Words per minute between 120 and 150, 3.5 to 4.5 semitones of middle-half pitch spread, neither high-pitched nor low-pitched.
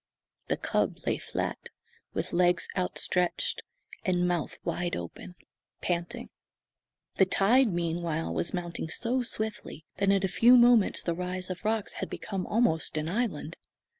Yes: average, 140 wpm; average, 4.0 semitones; medium, 180 Hz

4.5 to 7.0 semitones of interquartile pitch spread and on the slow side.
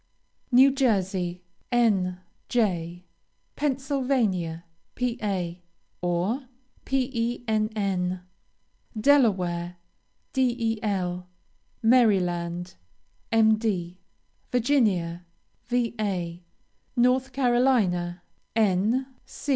Yes: wide, 5.5 semitones; slow, 50 wpm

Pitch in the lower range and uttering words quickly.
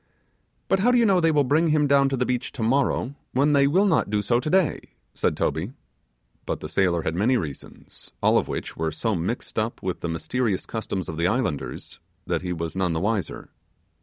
Yes: low, 115 Hz; fast, 210 wpm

